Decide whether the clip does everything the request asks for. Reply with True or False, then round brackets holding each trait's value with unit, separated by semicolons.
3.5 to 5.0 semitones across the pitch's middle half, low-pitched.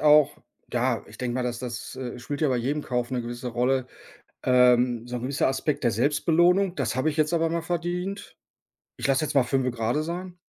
True (4.3 semitones; 130 Hz)